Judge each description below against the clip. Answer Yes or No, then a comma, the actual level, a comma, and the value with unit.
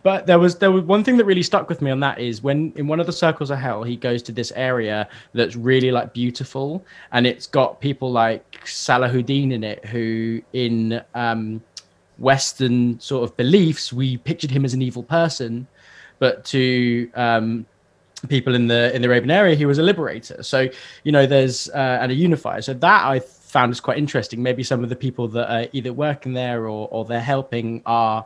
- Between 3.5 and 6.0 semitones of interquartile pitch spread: No, average, 2.8 semitones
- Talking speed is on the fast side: Yes, fast, 210 wpm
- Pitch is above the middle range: No, low, 125 Hz